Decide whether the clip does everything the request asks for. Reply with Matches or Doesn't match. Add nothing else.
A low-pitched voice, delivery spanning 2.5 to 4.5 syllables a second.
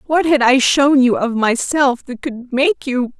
Doesn't match